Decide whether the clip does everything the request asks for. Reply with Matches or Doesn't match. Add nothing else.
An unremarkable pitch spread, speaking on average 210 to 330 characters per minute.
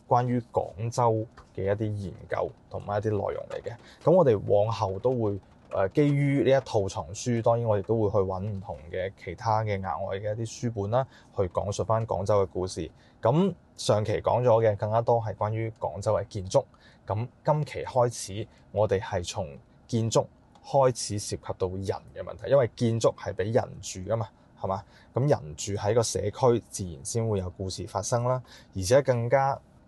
Matches